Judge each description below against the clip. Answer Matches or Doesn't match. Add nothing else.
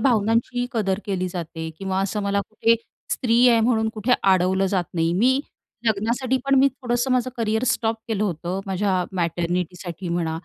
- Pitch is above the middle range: Matches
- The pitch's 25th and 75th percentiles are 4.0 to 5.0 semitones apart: Matches